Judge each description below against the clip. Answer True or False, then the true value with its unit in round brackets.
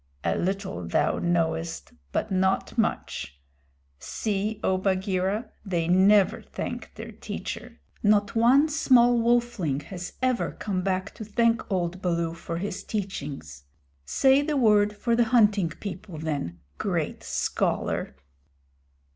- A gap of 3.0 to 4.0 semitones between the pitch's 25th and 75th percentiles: False (4.8 semitones)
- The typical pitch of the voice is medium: False (195 Hz)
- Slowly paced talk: True (125 wpm)